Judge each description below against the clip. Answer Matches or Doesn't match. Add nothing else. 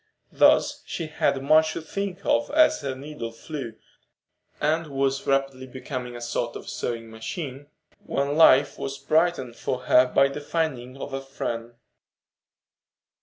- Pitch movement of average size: Matches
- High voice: Doesn't match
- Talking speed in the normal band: Matches